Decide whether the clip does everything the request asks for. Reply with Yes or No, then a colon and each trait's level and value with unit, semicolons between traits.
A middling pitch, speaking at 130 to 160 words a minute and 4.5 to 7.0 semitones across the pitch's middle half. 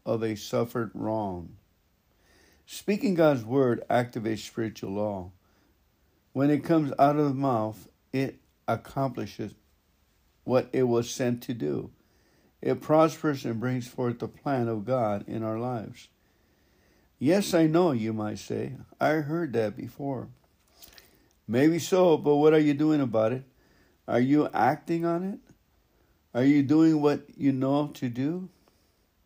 No: low, 125 Hz; average, 140 wpm; average, 5.2 semitones